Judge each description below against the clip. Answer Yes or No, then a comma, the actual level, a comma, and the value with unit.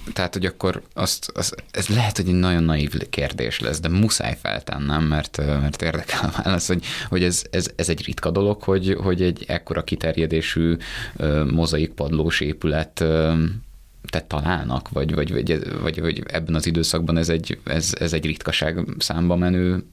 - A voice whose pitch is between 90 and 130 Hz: No, very low, 80 Hz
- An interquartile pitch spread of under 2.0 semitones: No, narrow, 2.5 semitones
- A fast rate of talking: Yes, fast, 160 wpm